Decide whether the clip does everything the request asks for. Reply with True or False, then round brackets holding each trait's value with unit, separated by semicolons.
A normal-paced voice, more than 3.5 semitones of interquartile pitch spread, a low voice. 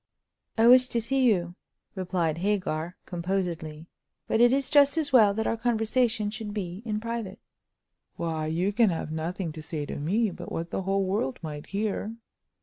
False (175 wpm; 5.2 semitones; 195 Hz)